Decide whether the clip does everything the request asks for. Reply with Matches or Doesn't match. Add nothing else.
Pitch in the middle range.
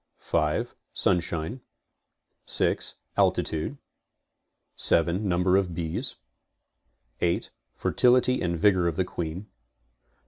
Doesn't match